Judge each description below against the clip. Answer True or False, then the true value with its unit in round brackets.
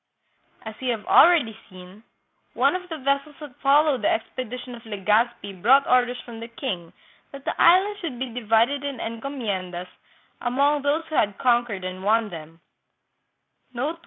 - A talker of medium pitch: False (245 Hz)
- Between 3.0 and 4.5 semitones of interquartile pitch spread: False (5.0 semitones)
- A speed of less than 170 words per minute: True (155 wpm)